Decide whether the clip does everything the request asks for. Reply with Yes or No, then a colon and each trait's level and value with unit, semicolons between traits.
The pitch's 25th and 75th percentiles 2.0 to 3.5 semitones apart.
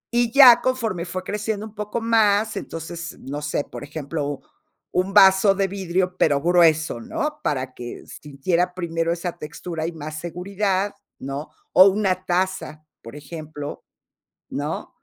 No: average, 4.4 semitones